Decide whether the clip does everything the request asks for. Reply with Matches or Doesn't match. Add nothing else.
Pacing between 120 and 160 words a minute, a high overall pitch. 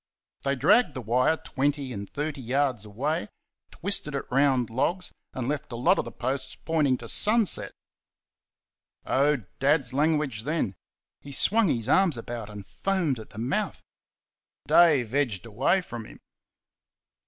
Doesn't match